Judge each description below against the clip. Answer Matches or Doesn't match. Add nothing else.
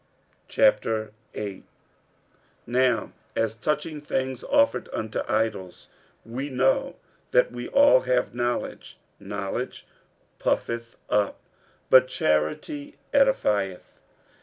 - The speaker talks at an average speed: Doesn't match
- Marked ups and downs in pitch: Matches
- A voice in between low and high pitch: Doesn't match